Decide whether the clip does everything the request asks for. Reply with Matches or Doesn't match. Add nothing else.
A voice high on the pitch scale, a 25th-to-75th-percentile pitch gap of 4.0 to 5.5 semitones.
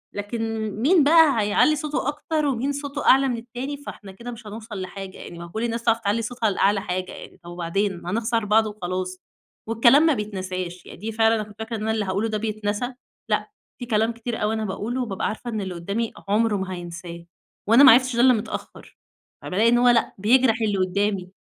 Doesn't match